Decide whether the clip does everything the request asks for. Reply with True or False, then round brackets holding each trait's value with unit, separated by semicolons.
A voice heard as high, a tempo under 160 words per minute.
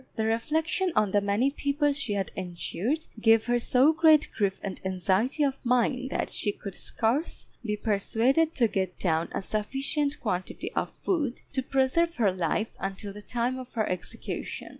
False (235 Hz; 170 wpm)